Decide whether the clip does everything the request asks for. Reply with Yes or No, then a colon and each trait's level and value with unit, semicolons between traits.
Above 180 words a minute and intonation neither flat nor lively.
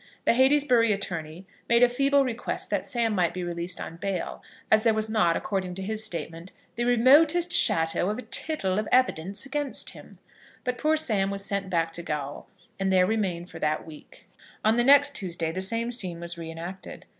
No: average, 195 wpm; wide, 5.9 semitones